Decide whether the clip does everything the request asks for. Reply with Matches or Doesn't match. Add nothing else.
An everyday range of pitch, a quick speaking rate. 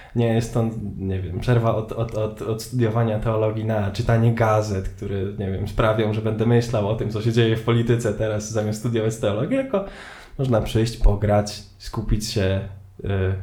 Doesn't match